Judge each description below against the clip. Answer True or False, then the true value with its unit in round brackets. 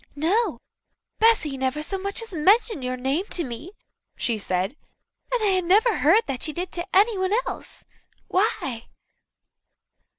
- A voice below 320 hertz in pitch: False (355 Hz)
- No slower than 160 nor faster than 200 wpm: False (140 wpm)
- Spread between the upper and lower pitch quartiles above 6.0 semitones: True (7.2 semitones)